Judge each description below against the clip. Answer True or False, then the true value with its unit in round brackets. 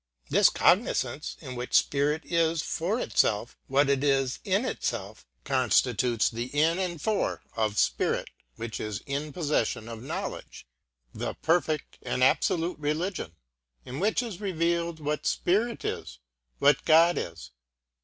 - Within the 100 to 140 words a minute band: True (135 wpm)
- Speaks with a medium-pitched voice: True (150 Hz)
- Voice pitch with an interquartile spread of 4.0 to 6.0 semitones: True (5.2 semitones)